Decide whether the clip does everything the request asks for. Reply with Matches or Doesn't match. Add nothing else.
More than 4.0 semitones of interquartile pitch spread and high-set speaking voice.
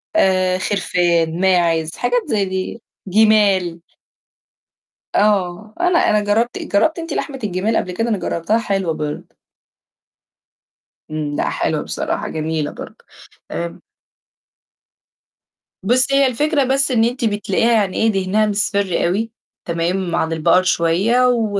Matches